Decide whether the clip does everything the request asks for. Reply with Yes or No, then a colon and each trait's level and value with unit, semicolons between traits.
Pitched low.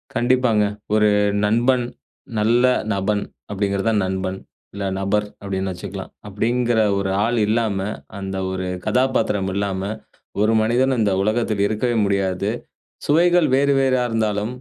Yes: low, 105 Hz